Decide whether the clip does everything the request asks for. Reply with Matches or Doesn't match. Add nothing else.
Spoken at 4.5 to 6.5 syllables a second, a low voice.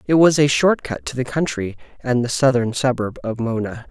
Matches